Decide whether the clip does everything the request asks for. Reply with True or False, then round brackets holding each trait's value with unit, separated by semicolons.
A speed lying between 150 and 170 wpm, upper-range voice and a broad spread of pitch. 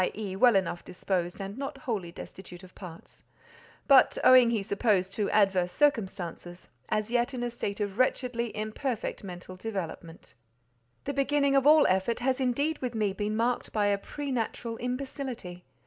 False (160 wpm; 220 Hz; 5.0 semitones)